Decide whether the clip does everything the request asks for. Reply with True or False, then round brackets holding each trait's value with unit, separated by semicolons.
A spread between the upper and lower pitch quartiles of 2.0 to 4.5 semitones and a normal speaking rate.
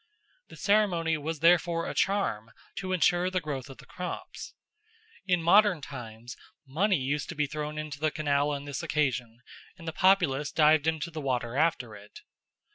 True (3.9 semitones; 170 wpm)